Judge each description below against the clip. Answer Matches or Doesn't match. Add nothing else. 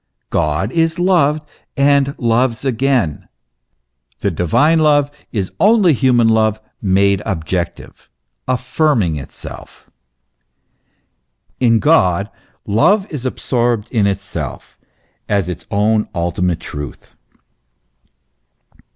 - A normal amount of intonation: Doesn't match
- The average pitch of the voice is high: Doesn't match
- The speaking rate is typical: Doesn't match